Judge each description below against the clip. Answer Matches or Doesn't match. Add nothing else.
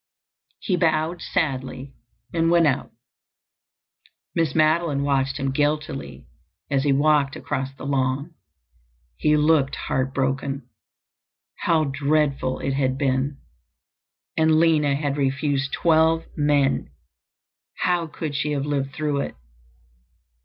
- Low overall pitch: Doesn't match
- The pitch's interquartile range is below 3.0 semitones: Matches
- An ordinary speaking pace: Doesn't match